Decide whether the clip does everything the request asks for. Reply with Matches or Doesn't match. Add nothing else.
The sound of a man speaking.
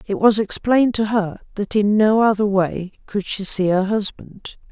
Doesn't match